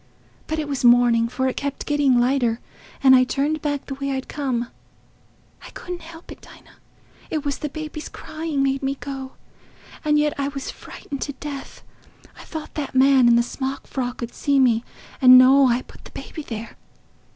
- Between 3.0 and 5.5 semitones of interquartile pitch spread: No, narrow, 2.4 semitones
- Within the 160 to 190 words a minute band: Yes, average, 185 wpm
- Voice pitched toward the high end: Yes, very high, 275 Hz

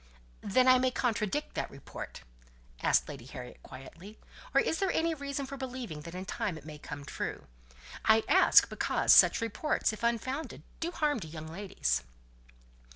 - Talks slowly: No, average, 165 wpm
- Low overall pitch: No, high, 220 Hz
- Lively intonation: Yes, wide, 8.9 semitones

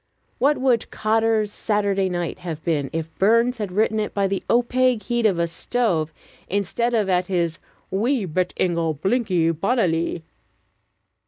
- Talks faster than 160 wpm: No, average, 150 wpm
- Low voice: No, high, 195 Hz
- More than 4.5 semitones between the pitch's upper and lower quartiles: Yes, average, 5.1 semitones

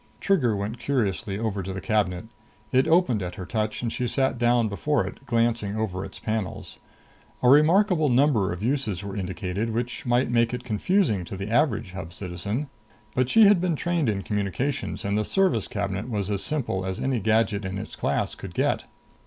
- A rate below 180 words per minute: No, average, 190 wpm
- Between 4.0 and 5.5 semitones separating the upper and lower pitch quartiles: Yes, average, 4.8 semitones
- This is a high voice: No, low, 110 Hz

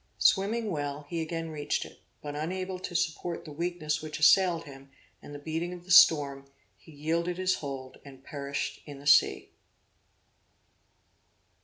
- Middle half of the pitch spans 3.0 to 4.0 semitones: Yes, average, 3.3 semitones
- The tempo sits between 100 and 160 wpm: Yes, average, 155 wpm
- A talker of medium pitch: Yes, medium, 155 Hz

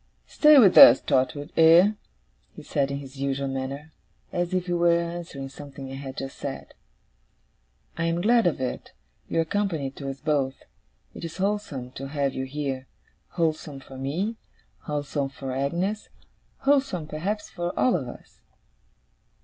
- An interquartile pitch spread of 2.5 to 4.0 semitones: No, average, 4.4 semitones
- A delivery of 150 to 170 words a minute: Yes, average, 160 wpm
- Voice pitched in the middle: Yes, medium, 150 Hz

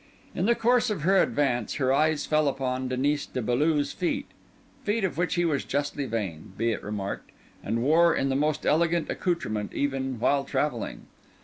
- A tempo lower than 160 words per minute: No, average, 175 wpm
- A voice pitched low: No, medium, 145 Hz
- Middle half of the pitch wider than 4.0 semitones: Yes, average, 4.5 semitones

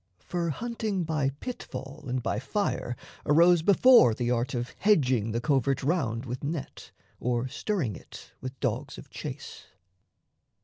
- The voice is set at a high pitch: No, low, 135 Hz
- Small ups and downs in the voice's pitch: No, wide, 5.5 semitones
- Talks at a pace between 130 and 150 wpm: Yes, average, 145 wpm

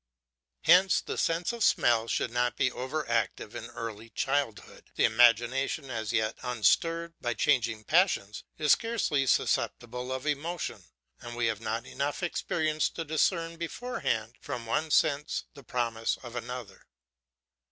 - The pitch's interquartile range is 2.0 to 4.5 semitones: No, average, 5.3 semitones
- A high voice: No, low, 125 Hz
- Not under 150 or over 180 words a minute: No, average, 140 wpm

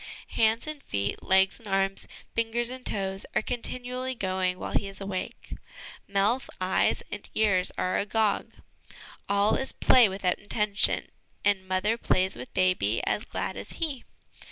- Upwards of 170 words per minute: No, average, 150 wpm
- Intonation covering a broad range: No, average, 3.5 semitones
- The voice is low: No, high, 200 Hz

